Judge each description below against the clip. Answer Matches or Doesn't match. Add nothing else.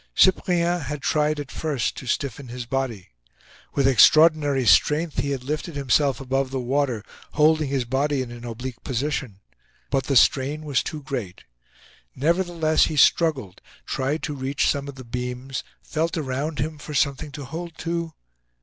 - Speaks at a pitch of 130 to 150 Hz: Matches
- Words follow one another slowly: Doesn't match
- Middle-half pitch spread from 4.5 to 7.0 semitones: Doesn't match